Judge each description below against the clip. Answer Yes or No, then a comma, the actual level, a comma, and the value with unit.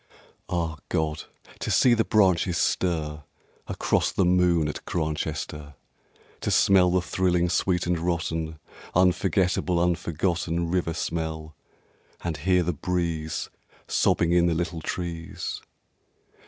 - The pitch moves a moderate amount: No, narrow, 1.9 semitones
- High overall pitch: No, very low, 85 Hz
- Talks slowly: Yes, slow, 115 wpm